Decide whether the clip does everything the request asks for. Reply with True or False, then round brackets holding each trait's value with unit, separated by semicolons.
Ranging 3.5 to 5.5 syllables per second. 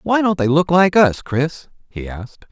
True (4.6 syllables/s)